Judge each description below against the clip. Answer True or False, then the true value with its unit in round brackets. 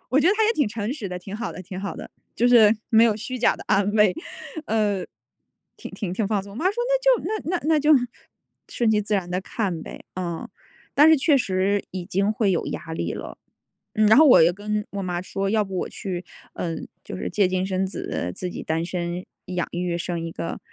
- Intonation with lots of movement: False (3.5 semitones)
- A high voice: True (200 Hz)